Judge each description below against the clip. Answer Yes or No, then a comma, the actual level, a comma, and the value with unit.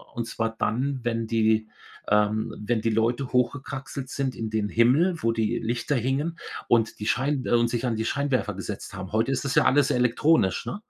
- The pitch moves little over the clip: No, average, 3.2 semitones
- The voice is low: Yes, low, 120 Hz